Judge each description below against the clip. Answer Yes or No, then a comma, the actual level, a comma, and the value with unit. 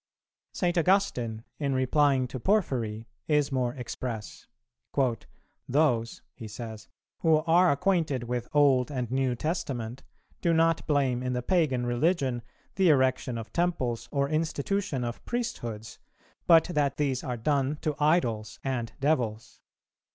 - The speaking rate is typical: No, slow, 130 wpm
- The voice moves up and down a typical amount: Yes, average, 4.4 semitones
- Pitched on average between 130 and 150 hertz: Yes, low, 135 Hz